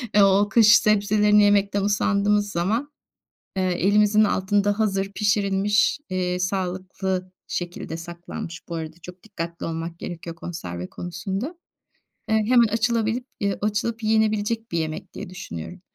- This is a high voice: Yes, high, 200 Hz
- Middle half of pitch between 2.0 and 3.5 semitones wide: Yes, average, 2.9 semitones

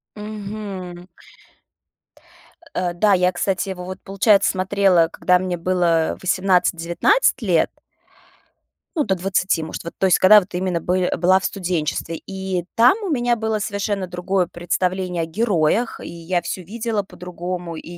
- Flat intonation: Yes, narrow, 2.3 semitones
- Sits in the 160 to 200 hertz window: Yes, medium, 185 Hz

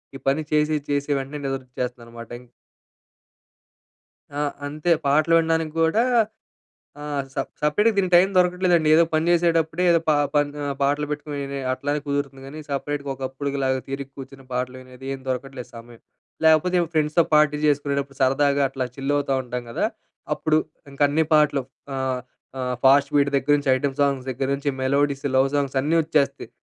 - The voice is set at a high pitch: No, medium, 140 Hz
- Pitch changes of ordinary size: No, narrow, 2.3 semitones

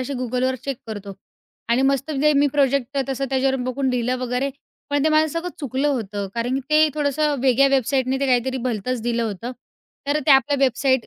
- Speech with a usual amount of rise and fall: No, narrow, 2.2 semitones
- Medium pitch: No, very high, 265 Hz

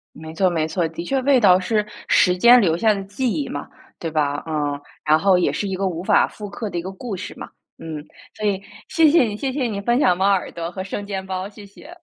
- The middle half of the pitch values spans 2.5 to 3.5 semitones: No, average, 4.0 semitones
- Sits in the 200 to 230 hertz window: No, high, 190 Hz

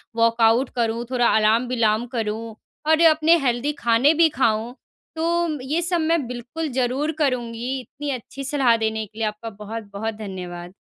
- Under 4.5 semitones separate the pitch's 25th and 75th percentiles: Yes, average, 4.0 semitones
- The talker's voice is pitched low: No, high, 240 Hz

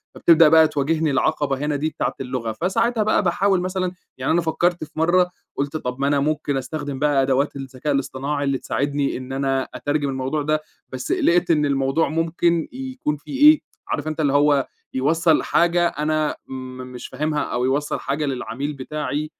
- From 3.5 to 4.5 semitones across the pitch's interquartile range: No, average, 3.1 semitones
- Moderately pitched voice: Yes, medium, 150 Hz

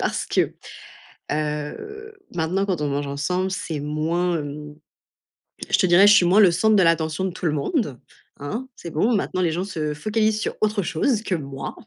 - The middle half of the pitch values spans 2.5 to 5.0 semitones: No, wide, 5.4 semitones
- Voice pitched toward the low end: No, medium, 175 Hz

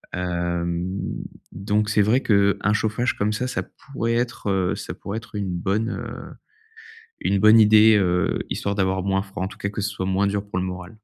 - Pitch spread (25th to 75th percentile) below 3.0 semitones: Yes, narrow, 2.4 semitones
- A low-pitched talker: Yes, low, 100 Hz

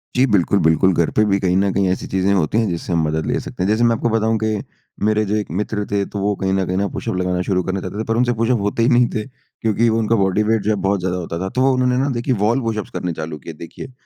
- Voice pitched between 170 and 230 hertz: No, low, 100 Hz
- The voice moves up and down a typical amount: Yes, average, 3.4 semitones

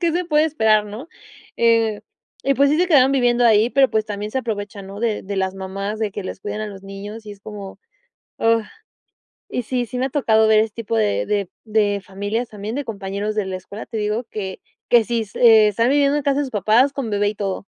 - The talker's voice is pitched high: Yes, high, 215 Hz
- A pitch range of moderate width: Yes, average, 3.1 semitones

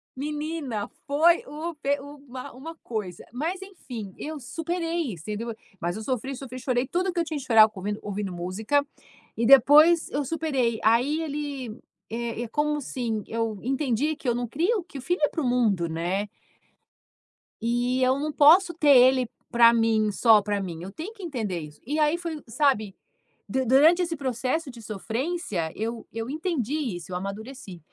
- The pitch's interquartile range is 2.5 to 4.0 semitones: No, wide, 5.5 semitones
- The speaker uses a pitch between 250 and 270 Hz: Yes, very high, 255 Hz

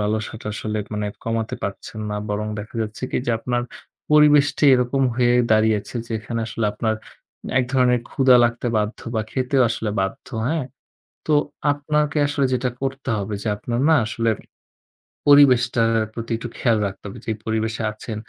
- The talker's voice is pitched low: Yes, low, 115 Hz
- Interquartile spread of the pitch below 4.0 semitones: Yes, average, 3.2 semitones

